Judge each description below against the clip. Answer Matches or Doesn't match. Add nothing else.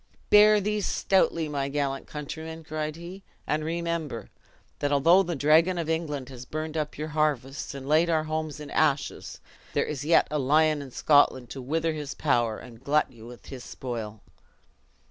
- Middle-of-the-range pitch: Matches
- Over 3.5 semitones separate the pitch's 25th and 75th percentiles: Doesn't match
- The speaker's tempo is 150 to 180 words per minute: Matches